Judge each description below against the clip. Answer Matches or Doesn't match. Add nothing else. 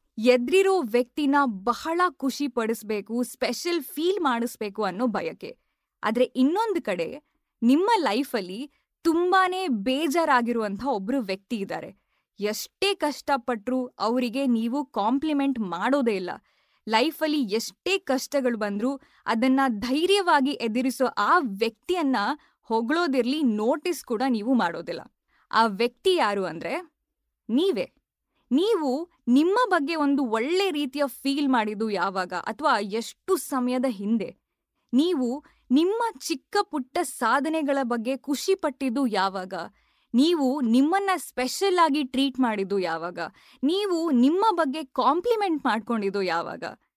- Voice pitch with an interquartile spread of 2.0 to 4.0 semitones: Doesn't match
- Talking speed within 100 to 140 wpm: Matches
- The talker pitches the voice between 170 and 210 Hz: Doesn't match